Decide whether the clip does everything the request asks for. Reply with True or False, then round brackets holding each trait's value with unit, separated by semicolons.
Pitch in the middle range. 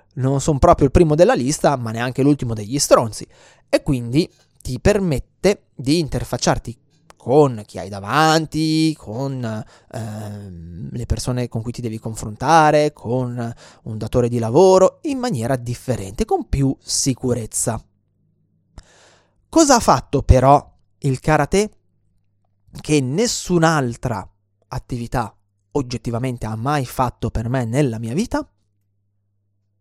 False (125 Hz)